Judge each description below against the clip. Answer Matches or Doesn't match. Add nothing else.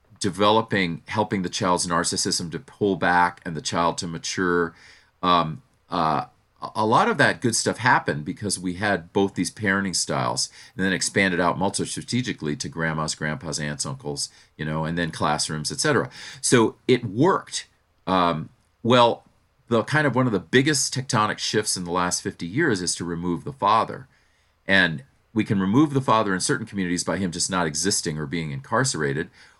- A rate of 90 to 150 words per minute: Doesn't match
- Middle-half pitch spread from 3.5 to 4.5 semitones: Matches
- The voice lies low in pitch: Matches